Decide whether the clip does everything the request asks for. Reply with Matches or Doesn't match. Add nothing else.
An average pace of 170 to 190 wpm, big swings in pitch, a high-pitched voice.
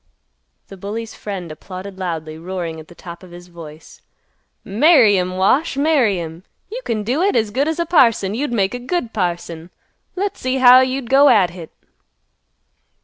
Matches